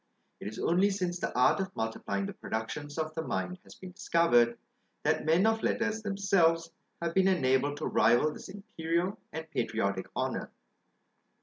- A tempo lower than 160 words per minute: No, average, 165 wpm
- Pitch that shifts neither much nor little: No, wide, 6.4 semitones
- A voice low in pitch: No, medium, 165 Hz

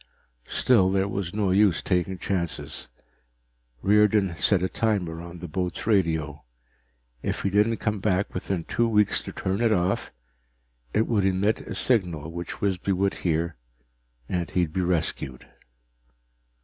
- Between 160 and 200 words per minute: No, average, 145 wpm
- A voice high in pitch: No, very low, 95 Hz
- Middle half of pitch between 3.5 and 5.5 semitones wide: No, average, 3.0 semitones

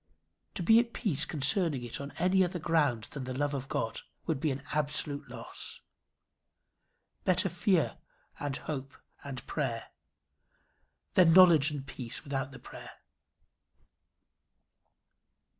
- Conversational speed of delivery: No, slow, 125 wpm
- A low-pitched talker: No, medium, 145 Hz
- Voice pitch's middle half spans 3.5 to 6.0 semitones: Yes, average, 4.2 semitones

